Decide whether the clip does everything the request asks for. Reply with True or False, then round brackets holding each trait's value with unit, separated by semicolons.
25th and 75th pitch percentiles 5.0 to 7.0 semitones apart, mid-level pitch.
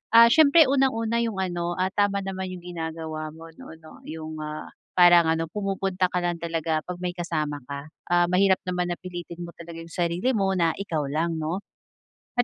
False (2.9 semitones; 175 Hz)